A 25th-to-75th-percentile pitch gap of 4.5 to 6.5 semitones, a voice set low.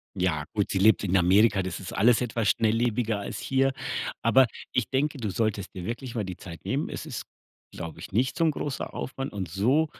Yes: average, 4.8 semitones; low, 110 Hz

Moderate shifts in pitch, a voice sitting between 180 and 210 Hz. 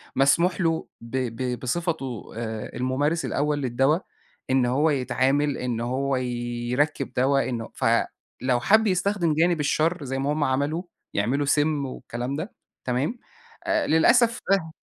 No: average, 4.2 semitones; medium, 140 Hz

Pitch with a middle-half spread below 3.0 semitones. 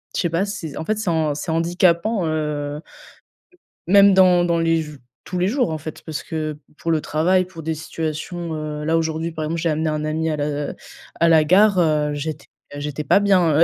Yes: narrow, 2.4 semitones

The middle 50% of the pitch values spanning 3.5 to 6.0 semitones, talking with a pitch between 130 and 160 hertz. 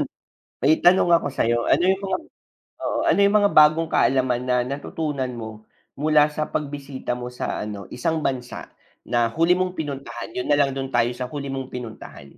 Yes: average, 4.0 semitones; low, 135 Hz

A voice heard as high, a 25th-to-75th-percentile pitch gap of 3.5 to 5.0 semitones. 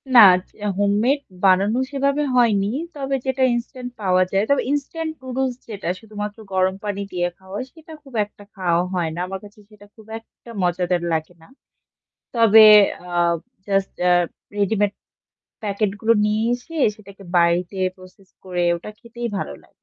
Yes: high, 205 Hz; average, 4.4 semitones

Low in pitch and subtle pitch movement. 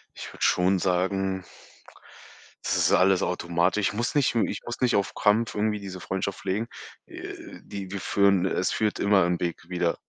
Yes: very low, 95 Hz; narrow, 2.3 semitones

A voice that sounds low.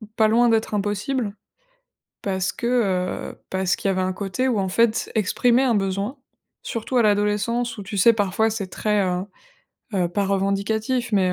No: high, 210 Hz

